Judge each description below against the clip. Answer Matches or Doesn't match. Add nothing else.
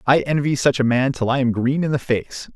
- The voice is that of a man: Matches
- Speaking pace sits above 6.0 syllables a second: Doesn't match